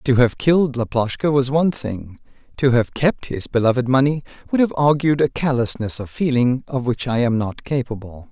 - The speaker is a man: Yes, male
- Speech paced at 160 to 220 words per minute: Yes, average, 190 wpm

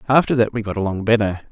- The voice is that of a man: Yes, male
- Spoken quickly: Yes, fast, 235 wpm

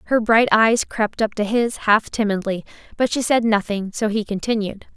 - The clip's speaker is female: Yes, female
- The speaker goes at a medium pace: Yes, average, 195 wpm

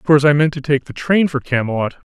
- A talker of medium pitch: Yes, medium, 145 Hz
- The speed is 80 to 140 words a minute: No, fast, 285 wpm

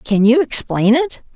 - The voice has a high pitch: Yes, very high, 250 Hz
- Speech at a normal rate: Yes, average, 175 wpm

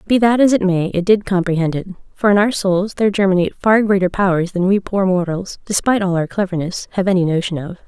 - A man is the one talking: No, female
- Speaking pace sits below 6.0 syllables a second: No, 6.2 syllables/s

